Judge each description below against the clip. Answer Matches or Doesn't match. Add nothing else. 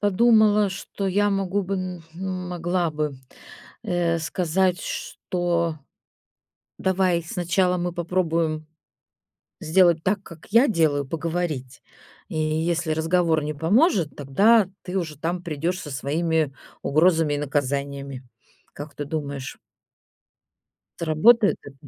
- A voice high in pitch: Doesn't match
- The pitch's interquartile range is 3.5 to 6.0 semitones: Doesn't match